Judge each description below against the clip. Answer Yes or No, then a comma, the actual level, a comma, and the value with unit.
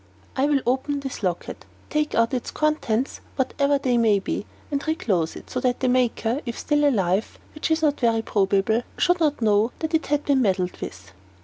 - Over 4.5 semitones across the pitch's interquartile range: Yes, average, 5.0 semitones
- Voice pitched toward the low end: No, very high, 250 Hz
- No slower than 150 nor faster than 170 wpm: No, average, 195 wpm